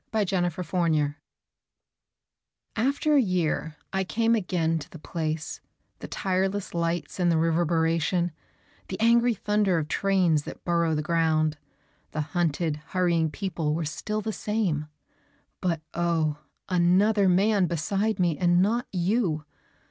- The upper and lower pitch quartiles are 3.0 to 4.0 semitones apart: Yes, average, 3.5 semitones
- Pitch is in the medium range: Yes, medium, 175 Hz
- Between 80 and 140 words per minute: Yes, slow, 135 wpm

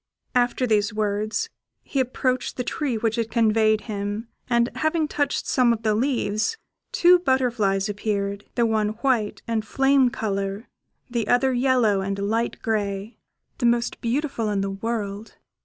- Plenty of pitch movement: No, average, 3.3 semitones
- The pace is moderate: Yes, average, 150 wpm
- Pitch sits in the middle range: No, high, 225 Hz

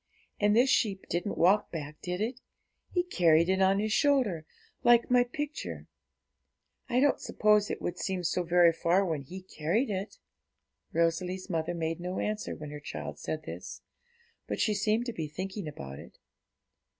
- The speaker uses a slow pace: No, average, 170 wpm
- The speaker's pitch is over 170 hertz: Yes, medium, 185 Hz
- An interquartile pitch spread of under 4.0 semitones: No, average, 4.4 semitones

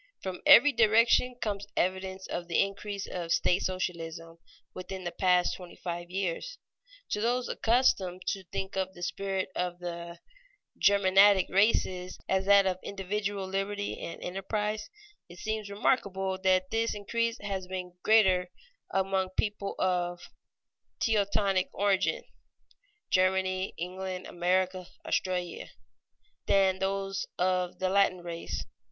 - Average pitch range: No, narrow, 1.8 semitones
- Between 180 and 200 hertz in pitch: Yes, high, 190 Hz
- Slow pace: Yes, slow, 125 wpm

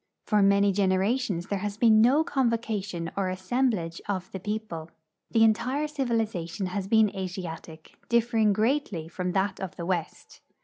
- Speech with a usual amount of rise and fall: Yes, average, 3.6 semitones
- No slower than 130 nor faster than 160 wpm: Yes, average, 150 wpm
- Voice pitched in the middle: No, high, 200 Hz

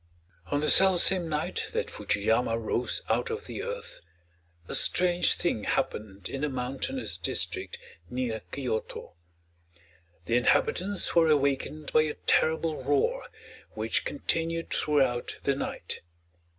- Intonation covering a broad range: Yes, wide, 6.0 semitones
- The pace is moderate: No, slow, 130 wpm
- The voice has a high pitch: No, medium, 150 Hz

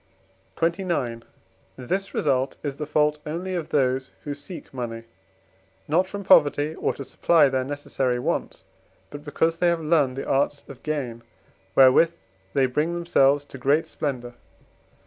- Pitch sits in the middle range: Yes, medium, 145 Hz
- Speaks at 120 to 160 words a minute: Yes, average, 145 wpm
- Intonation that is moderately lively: Yes, average, 3.7 semitones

